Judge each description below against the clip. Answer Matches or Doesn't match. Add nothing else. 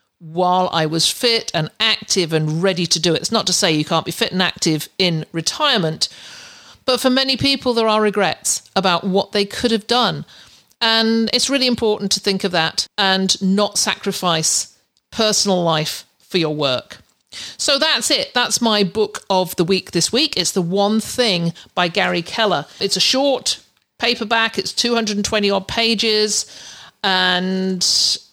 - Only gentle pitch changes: Doesn't match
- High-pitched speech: Matches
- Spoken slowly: Doesn't match